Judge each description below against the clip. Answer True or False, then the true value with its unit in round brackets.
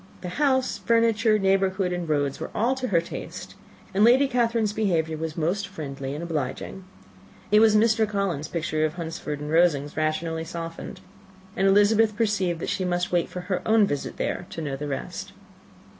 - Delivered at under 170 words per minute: False (175 wpm)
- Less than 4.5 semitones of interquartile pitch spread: False (5.0 semitones)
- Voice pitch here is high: False (180 Hz)